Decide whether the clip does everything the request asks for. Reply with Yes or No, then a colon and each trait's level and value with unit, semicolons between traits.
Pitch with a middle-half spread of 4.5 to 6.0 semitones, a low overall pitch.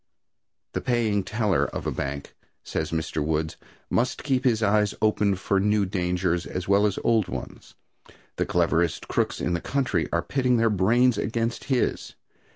Yes: average, 4.8 semitones; low, 100 Hz